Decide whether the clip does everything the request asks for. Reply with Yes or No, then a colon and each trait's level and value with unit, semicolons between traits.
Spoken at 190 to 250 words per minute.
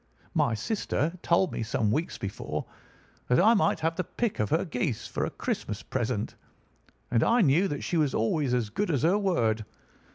Yes: average, 195 wpm